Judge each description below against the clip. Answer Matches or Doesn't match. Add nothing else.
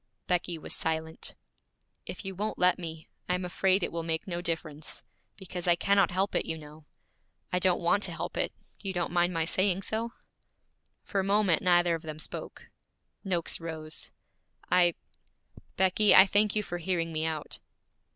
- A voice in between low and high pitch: Matches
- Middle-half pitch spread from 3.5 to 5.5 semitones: Doesn't match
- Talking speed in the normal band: Matches